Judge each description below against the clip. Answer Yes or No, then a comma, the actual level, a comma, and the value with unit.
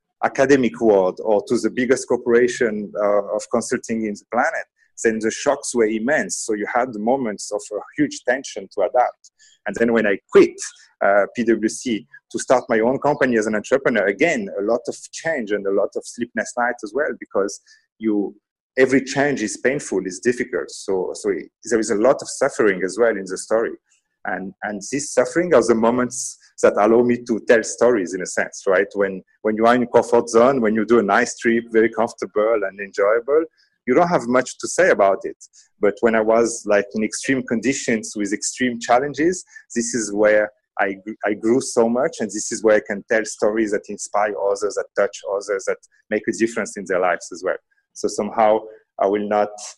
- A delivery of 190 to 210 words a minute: Yes, fast, 205 wpm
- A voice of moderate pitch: No, low, 120 Hz